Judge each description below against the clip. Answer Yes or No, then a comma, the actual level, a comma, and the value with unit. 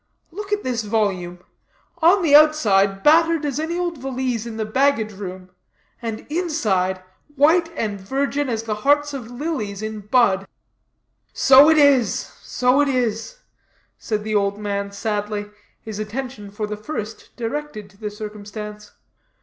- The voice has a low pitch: No, high, 225 Hz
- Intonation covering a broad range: Yes, wide, 5.7 semitones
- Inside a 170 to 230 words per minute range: No, average, 150 wpm